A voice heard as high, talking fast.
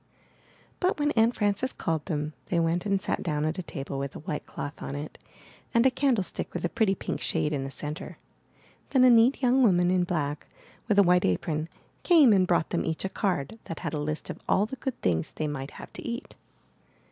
No: medium, 180 Hz; fast, 225 wpm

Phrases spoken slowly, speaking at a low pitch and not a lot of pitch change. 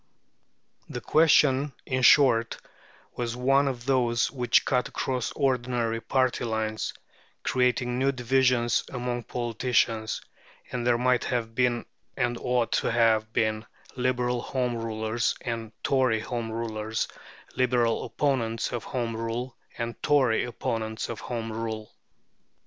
Yes: slow, 125 wpm; low, 120 Hz; narrow, 1.9 semitones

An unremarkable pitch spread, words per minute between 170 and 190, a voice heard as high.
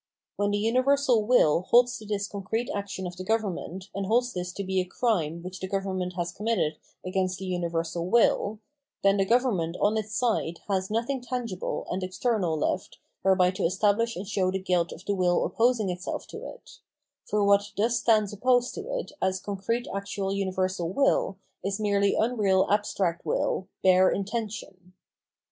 Yes: average, 3.3 semitones; average, 175 wpm; high, 200 Hz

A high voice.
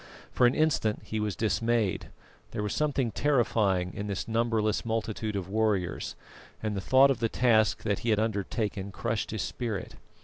No: low, 110 Hz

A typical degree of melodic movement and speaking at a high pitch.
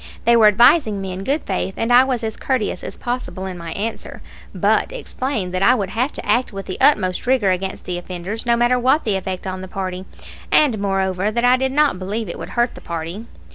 Yes: average, 4.7 semitones; high, 210 Hz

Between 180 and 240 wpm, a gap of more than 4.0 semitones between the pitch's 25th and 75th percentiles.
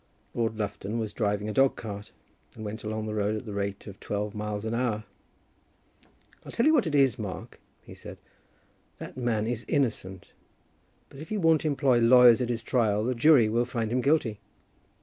No: average, 190 wpm; average, 3.3 semitones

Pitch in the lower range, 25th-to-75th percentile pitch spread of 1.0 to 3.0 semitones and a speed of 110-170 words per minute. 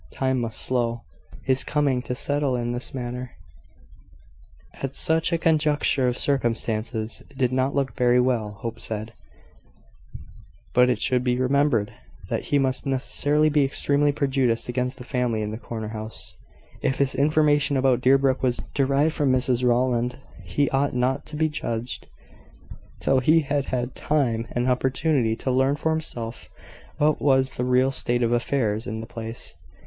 Yes: low, 130 Hz; average, 2.7 semitones; average, 160 wpm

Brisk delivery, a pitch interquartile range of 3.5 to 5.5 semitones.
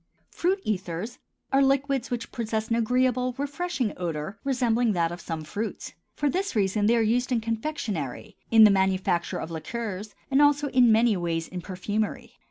No: average, 170 wpm; average, 5.1 semitones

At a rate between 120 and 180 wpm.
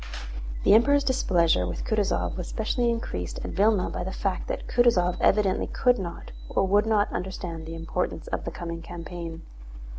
Yes: average, 170 wpm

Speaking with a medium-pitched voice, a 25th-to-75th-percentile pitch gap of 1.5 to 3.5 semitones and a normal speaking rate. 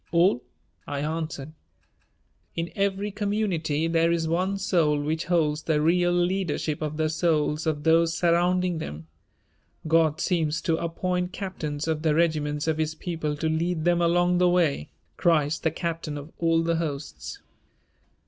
Yes: medium, 165 Hz; narrow, 2.4 semitones; average, 150 wpm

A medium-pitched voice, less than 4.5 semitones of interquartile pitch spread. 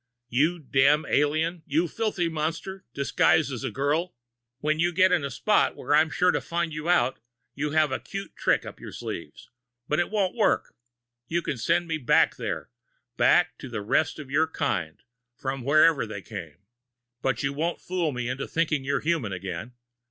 Yes: medium, 155 Hz; average, 4.1 semitones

